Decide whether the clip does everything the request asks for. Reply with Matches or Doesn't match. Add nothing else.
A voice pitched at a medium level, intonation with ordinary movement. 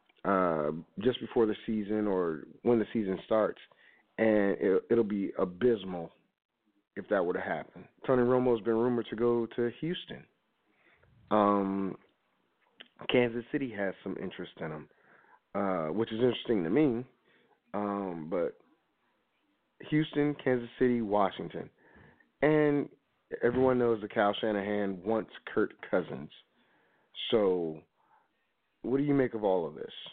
Doesn't match